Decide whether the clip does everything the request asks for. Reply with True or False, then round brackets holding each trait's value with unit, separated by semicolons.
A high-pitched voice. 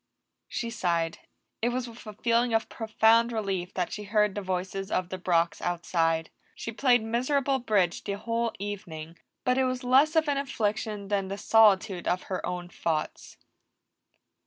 True (210 Hz)